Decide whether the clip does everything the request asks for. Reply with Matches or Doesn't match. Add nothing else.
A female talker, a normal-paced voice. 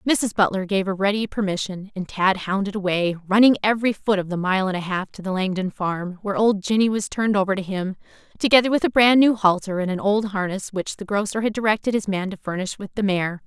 Doesn't match